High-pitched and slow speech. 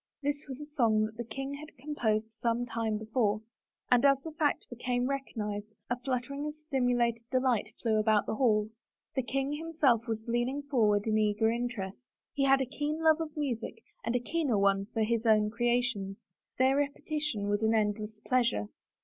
No: high, 240 Hz; average, 185 wpm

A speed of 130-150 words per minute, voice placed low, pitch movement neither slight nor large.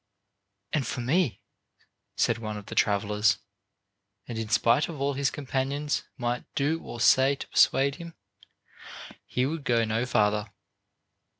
Yes: average, 140 wpm; low, 125 Hz; average, 4.1 semitones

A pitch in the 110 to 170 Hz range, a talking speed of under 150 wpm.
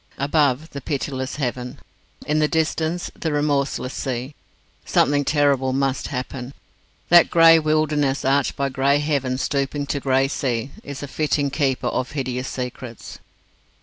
Yes: medium, 140 Hz; average, 140 wpm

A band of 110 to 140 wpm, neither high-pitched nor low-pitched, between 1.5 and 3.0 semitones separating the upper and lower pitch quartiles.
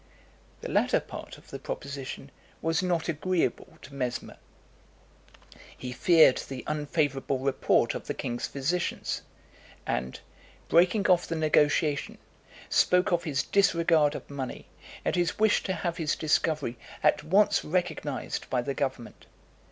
No: slow, 135 wpm; medium, 155 Hz; average, 4.1 semitones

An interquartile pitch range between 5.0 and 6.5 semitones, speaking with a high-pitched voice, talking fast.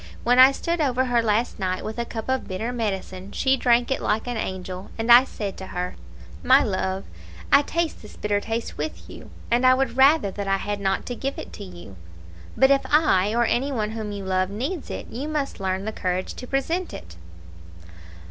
Yes: average, 5.3 semitones; high, 225 Hz; fast, 210 wpm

